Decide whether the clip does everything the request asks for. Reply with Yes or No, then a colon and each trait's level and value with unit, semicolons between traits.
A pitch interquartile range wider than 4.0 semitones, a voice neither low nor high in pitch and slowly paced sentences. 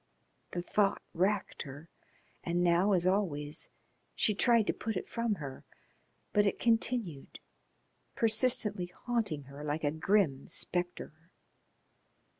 Yes: average, 5.3 semitones; medium, 180 Hz; slow, 120 wpm